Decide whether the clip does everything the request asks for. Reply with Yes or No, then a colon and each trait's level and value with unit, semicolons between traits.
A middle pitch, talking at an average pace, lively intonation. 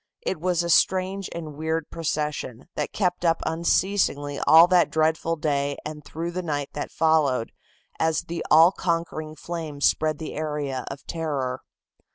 No: medium, 160 Hz; average, 155 wpm; narrow, 2.5 semitones